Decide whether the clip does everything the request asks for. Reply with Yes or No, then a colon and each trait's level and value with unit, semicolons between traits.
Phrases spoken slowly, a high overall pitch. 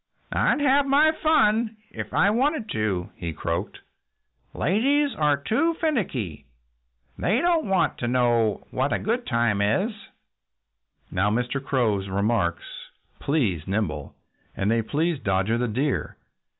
No: slow, 125 wpm; low, 130 Hz